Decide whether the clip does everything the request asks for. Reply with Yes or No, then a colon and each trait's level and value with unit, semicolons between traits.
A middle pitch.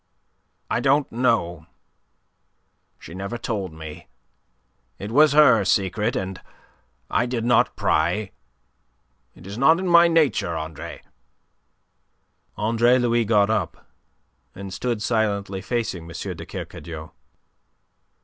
No: low, 110 Hz